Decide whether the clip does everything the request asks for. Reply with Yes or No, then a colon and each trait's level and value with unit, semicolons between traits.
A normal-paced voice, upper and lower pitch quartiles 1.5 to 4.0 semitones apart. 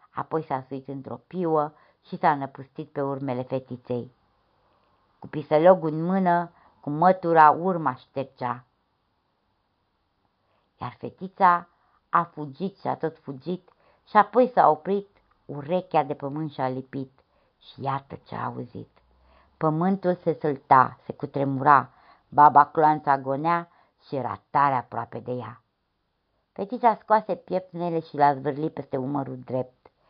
No: average, 130 wpm; average, 4.9 semitones